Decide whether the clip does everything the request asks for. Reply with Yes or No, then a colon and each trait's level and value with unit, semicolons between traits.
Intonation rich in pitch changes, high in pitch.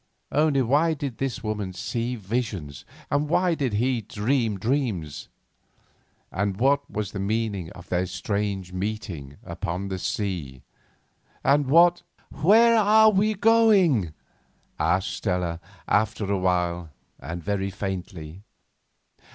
No: wide, 7.3 semitones; low, 105 Hz